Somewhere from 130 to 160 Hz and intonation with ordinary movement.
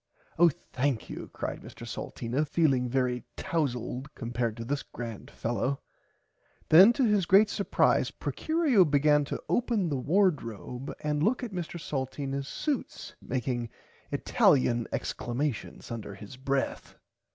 No: medium, 140 Hz; wide, 5.8 semitones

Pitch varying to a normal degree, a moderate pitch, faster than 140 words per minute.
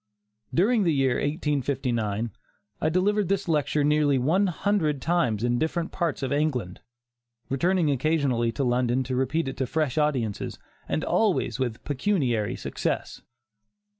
No: average, 4.7 semitones; medium, 145 Hz; slow, 135 wpm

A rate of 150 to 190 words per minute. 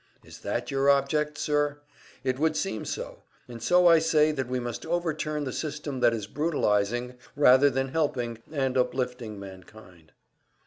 Yes: average, 160 wpm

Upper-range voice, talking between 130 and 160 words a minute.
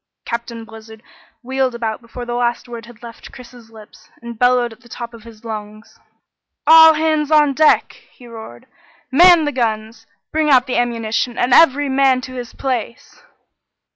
No: high, 240 Hz; average, 170 wpm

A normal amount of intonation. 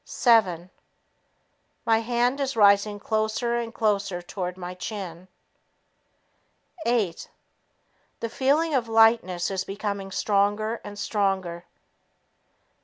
Yes: average, 3.3 semitones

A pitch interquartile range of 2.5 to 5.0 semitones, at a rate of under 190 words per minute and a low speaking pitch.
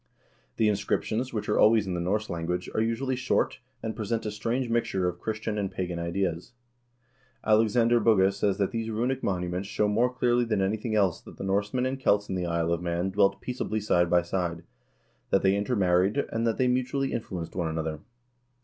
No: average, 4.1 semitones; average, 195 wpm; low, 105 Hz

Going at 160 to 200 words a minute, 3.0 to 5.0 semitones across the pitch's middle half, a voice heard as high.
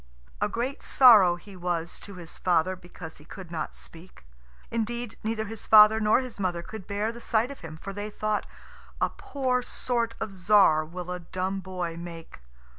Yes: average, 185 wpm; average, 4.2 semitones; high, 195 Hz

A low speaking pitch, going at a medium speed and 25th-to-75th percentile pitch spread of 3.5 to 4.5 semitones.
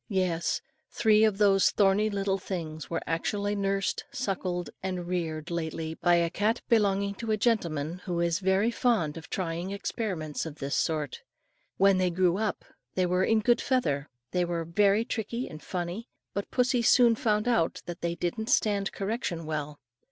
No: high, 190 Hz; average, 170 wpm; average, 3.9 semitones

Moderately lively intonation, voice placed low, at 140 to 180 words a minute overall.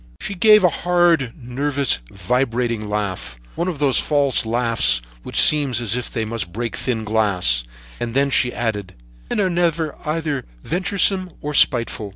No: wide, 5.7 semitones; low, 125 Hz; average, 160 wpm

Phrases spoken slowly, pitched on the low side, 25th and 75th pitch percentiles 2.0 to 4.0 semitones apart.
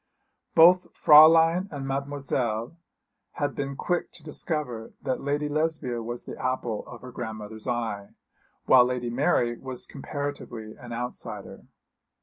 Yes: slow, 130 wpm; low, 130 Hz; average, 3.7 semitones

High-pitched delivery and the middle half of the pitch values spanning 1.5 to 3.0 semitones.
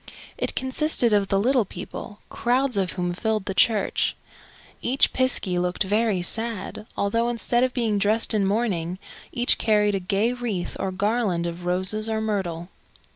No: high, 210 Hz; average, 3.7 semitones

